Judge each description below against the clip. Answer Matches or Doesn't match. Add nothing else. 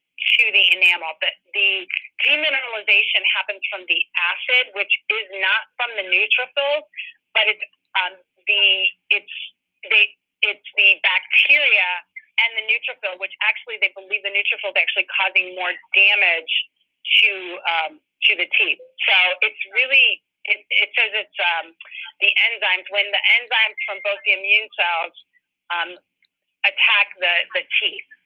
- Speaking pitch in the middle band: Doesn't match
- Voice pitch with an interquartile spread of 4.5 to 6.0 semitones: Doesn't match